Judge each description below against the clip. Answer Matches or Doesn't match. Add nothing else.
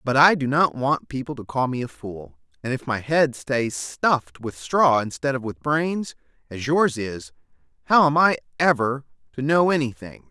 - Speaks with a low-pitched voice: Matches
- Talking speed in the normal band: Matches